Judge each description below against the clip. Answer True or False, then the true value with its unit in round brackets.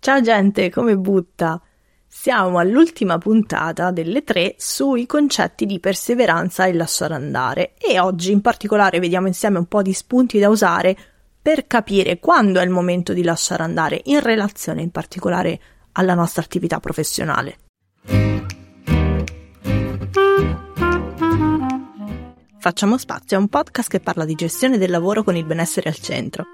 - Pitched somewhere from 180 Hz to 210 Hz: True (185 Hz)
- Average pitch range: True (4.4 semitones)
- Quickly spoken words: False (140 wpm)